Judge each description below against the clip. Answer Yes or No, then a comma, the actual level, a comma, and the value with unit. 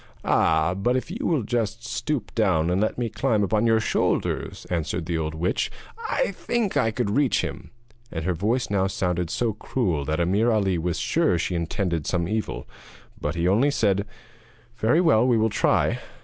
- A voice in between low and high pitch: No, low, 105 Hz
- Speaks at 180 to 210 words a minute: Yes, average, 190 wpm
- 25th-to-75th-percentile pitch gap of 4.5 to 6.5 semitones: Yes, average, 5.2 semitones